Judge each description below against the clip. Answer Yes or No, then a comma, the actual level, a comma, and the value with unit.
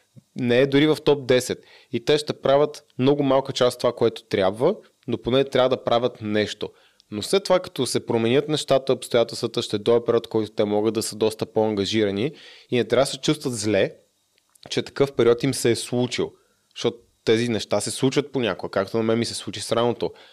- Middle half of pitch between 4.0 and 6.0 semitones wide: No, average, 3.4 semitones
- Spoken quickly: Yes, fast, 205 wpm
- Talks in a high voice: No, low, 120 Hz